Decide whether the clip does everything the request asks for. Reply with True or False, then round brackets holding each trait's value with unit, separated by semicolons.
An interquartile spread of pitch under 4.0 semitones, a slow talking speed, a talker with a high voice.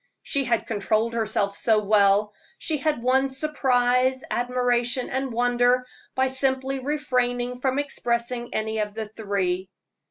True (3.1 semitones; 130 wpm; 245 Hz)